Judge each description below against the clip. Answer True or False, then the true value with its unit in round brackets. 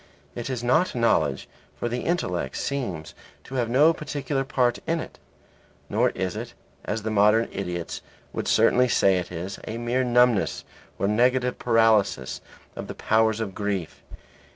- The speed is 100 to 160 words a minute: True (155 wpm)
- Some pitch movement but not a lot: True (4.1 semitones)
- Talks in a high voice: False (115 Hz)